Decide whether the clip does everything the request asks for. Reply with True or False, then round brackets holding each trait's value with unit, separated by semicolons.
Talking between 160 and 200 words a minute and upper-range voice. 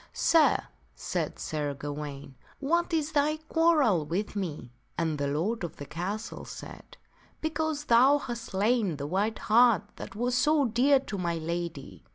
True (175 wpm; 210 Hz)